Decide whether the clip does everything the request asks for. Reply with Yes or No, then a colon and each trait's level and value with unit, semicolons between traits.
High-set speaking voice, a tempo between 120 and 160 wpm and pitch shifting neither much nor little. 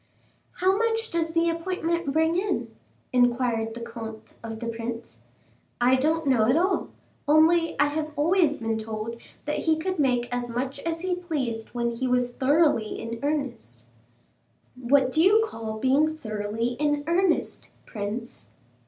No: very high, 270 Hz; average, 155 wpm; wide, 6.0 semitones